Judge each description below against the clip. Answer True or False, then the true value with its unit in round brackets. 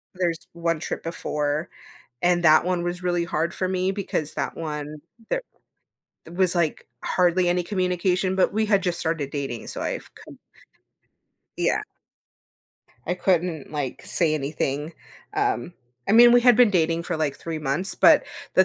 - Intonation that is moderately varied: True (3.0 semitones)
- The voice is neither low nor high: True (175 Hz)